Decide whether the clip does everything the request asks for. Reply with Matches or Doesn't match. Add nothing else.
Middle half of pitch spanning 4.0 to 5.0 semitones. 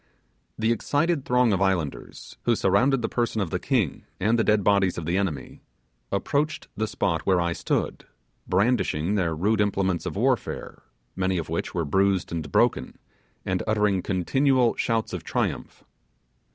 Matches